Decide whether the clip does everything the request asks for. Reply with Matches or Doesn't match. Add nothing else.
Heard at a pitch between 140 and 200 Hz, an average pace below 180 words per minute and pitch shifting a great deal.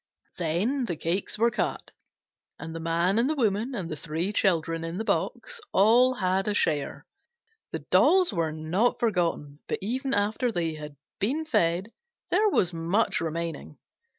Matches